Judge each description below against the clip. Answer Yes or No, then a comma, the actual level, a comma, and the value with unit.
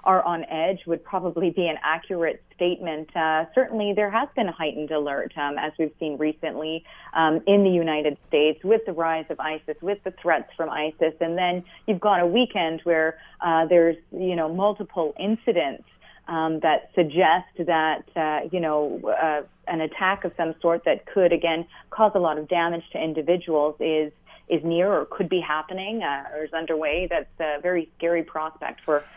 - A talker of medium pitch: Yes, medium, 165 Hz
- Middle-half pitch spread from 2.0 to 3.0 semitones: Yes, narrow, 2.6 semitones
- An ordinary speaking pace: Yes, average, 185 wpm